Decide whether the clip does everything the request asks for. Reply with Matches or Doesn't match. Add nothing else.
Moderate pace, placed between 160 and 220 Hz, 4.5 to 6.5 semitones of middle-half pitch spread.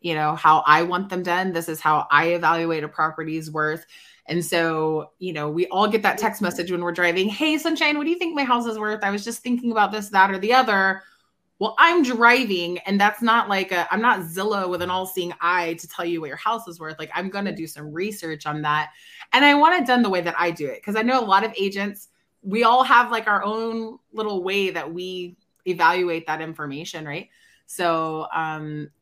Doesn't match